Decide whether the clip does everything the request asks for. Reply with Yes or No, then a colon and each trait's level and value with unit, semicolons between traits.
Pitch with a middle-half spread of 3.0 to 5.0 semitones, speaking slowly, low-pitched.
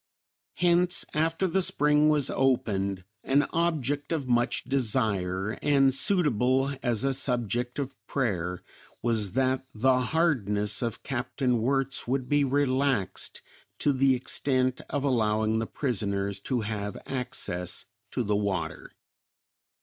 Yes: average, 4.5 semitones; slow, 125 wpm; low, 130 Hz